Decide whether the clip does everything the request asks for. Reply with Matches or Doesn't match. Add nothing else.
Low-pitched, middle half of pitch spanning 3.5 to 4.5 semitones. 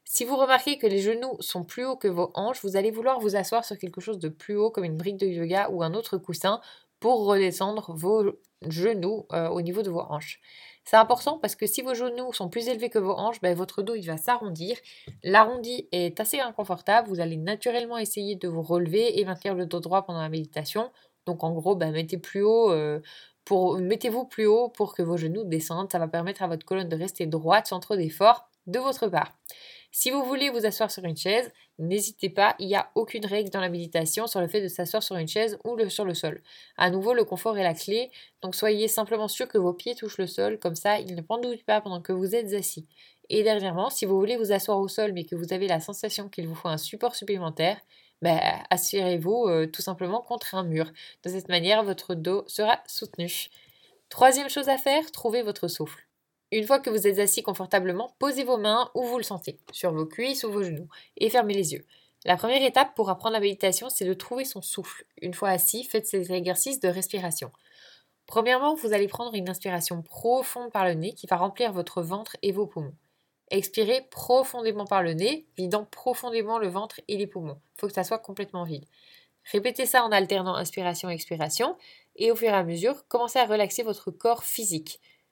Doesn't match